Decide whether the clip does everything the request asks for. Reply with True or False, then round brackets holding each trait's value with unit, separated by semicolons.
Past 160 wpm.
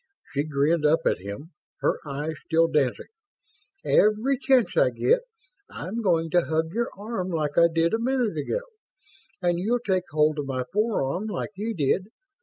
True (170 wpm)